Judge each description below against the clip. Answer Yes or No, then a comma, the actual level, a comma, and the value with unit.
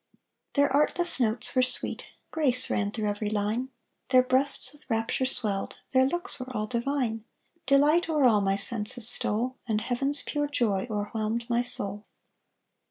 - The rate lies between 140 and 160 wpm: Yes, average, 155 wpm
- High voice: Yes, high, 245 Hz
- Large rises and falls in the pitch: No, average, 4.3 semitones